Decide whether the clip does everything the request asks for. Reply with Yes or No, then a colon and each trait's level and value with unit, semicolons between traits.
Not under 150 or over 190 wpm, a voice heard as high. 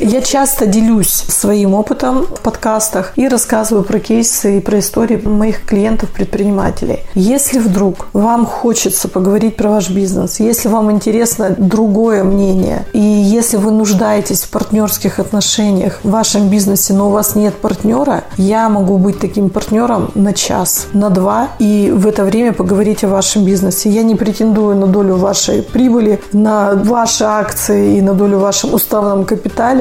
Yes: average, 155 wpm; high, 210 Hz